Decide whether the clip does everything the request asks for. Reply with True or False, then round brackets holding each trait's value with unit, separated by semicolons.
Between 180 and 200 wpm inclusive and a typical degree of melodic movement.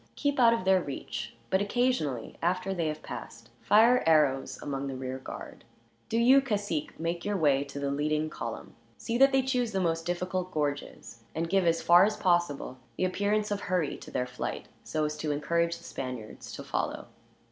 False (190 wpm; 5.7 semitones)